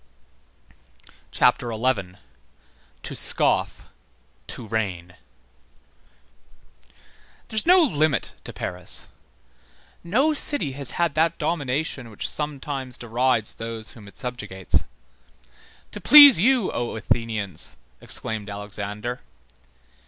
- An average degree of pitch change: No, wide, 6.8 semitones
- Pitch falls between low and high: No, low, 125 Hz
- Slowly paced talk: Yes, slow, 95 wpm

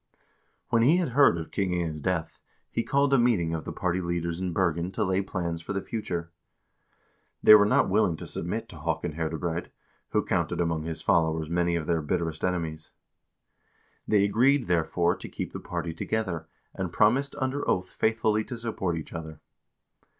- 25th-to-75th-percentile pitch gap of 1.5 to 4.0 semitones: No, average, 4.6 semitones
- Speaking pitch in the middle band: No, very low, 90 Hz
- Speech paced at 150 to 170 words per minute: No, average, 180 wpm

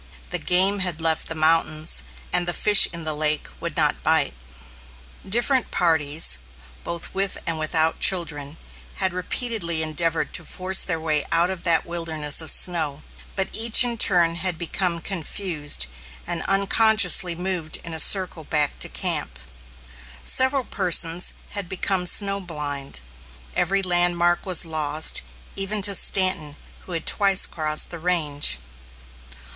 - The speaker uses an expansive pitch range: No, average, 3.3 semitones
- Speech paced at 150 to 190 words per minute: No, average, 140 wpm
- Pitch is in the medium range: Yes, medium, 170 Hz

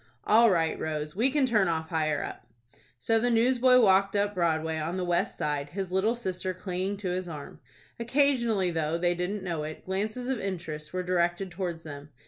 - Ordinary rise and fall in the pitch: Yes, average, 4.5 semitones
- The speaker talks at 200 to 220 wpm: No, average, 190 wpm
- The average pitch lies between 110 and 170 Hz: No, medium, 185 Hz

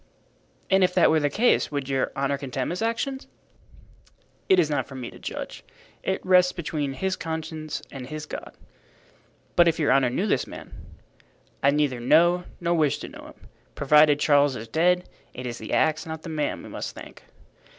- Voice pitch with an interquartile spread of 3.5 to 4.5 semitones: Yes, average, 3.9 semitones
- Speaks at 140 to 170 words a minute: No, average, 190 wpm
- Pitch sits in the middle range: Yes, medium, 155 Hz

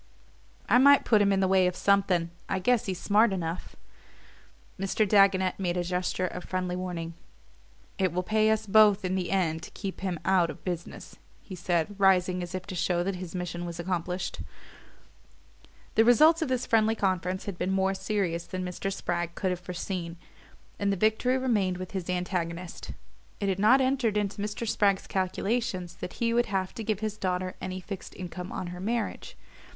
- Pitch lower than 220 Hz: Yes, high, 190 Hz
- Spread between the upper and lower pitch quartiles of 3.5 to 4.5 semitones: No, narrow, 2.6 semitones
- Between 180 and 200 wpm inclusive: Yes, average, 190 wpm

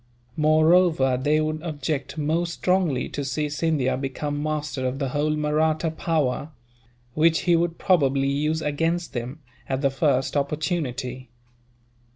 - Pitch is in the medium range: Yes, medium, 150 Hz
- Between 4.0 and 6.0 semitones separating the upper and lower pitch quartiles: No, average, 2.7 semitones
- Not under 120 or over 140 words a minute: Yes, slow, 135 wpm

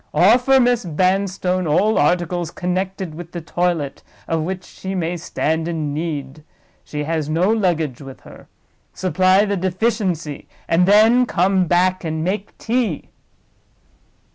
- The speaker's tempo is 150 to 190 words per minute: No, slow, 135 wpm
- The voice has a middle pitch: Yes, medium, 180 Hz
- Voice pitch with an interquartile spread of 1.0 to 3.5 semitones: Yes, average, 3.2 semitones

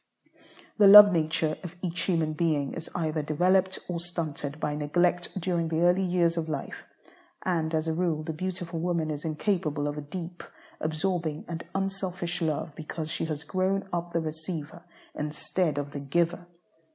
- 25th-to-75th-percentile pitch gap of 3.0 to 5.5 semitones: No, narrow, 2.4 semitones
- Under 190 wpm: Yes, average, 165 wpm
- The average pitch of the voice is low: No, medium, 165 Hz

